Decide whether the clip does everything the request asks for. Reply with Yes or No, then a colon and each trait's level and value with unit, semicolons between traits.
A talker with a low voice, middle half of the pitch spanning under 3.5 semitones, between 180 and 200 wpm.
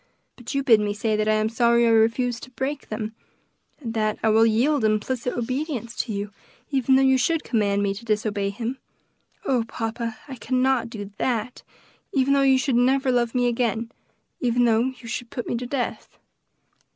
No: high, 235 Hz; average, 2.8 semitones; average, 190 wpm